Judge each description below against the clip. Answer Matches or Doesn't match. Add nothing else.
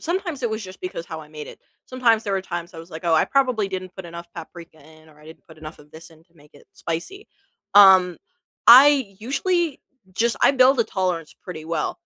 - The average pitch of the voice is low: Doesn't match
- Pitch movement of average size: Doesn't match